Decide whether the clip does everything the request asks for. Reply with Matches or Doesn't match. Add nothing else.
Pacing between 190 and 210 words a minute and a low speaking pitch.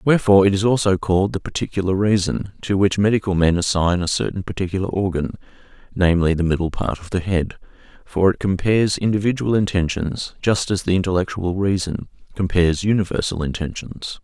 Doesn't match